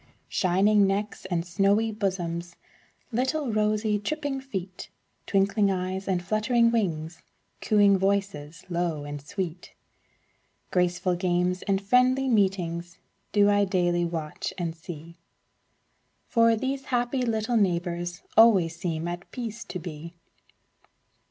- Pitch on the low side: No, high, 195 Hz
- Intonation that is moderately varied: Yes, average, 3.7 semitones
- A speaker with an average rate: No, slow, 115 wpm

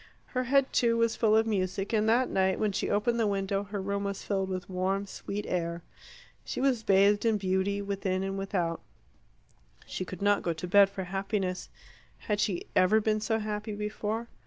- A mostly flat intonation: Yes, narrow, 2.2 semitones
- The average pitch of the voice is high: Yes, high, 200 Hz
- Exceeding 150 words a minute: Yes, average, 190 wpm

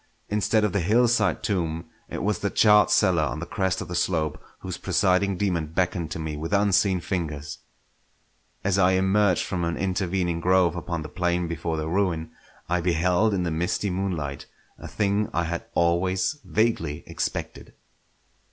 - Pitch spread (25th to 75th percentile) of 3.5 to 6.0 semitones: No, average, 2.9 semitones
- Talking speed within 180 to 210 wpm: No, average, 165 wpm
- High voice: No, very low, 90 Hz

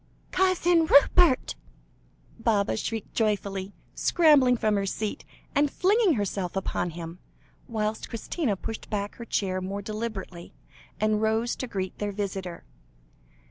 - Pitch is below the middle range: No, high, 215 Hz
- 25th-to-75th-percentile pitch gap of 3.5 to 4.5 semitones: Yes, average, 4.2 semitones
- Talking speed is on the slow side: Yes, slow, 125 wpm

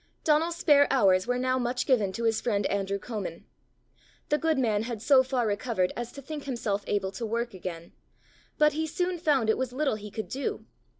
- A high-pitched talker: Yes, high, 240 Hz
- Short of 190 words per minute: No, average, 200 wpm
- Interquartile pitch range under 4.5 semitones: No, average, 5.3 semitones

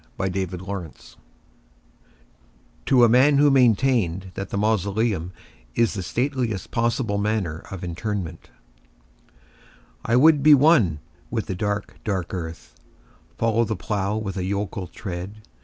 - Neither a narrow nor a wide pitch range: Yes, average, 3.9 semitones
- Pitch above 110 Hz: No, low, 105 Hz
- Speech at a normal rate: No, slow, 130 wpm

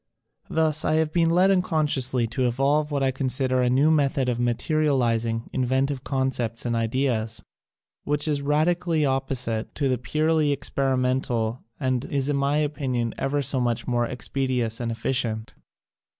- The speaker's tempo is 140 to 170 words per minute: Yes, average, 150 wpm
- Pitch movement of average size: Yes, average, 3.3 semitones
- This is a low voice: Yes, low, 130 Hz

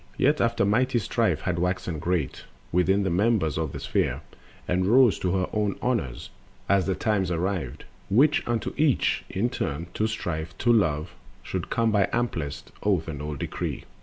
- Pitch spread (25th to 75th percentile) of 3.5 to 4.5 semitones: No, wide, 5.6 semitones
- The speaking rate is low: No, average, 170 wpm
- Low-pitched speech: Yes, very low, 95 Hz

